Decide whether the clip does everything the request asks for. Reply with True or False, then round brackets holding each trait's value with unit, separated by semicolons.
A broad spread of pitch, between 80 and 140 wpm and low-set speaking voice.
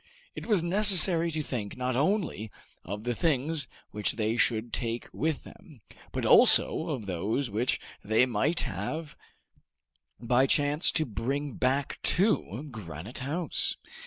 True (6.0 semitones; 135 wpm; 130 Hz)